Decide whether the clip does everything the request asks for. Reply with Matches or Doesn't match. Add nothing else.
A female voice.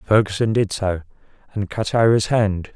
Doesn't match